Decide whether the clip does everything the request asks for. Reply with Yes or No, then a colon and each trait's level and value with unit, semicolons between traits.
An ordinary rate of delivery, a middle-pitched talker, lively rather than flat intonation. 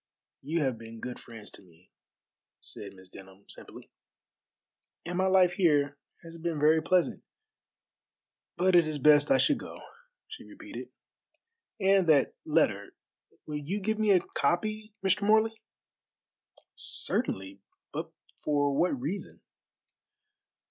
No: slow, 130 wpm; medium, 155 Hz; wide, 6.2 semitones